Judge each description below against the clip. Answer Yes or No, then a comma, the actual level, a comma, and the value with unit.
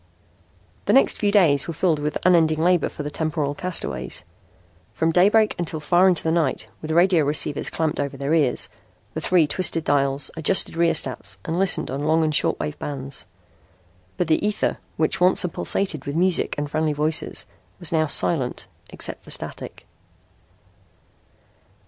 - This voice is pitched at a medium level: Yes, medium, 160 Hz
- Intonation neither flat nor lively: Yes, average, 3.3 semitones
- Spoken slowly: No, average, 165 wpm